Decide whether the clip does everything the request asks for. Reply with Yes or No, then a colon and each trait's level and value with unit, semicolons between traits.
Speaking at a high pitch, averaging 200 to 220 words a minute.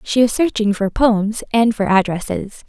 No: high, 215 Hz; average, 180 wpm